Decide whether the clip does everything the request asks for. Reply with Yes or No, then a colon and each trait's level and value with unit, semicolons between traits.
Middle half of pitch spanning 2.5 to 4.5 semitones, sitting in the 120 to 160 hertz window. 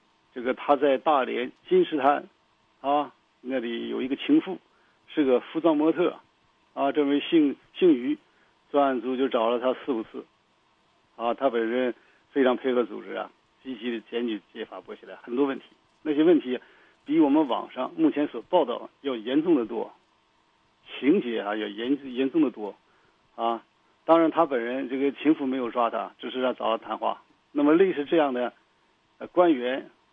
No: average, 5.3 semitones; medium, 140 Hz